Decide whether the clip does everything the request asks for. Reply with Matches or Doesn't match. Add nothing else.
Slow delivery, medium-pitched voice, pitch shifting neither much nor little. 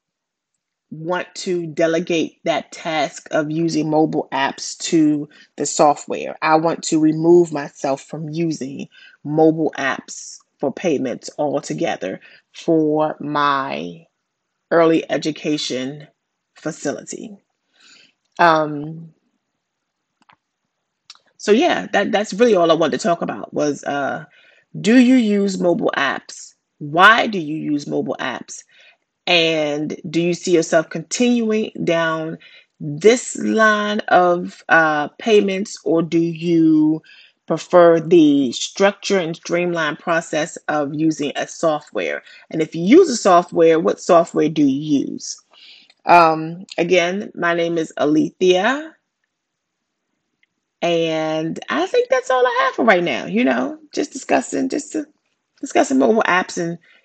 Matches